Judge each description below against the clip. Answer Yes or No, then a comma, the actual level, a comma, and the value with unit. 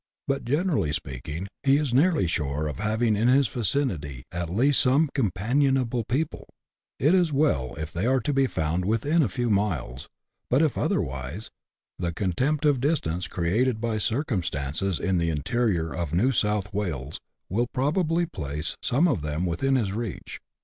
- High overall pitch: No, low, 110 Hz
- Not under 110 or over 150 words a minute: No, average, 170 wpm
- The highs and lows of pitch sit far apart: Yes, wide, 8.3 semitones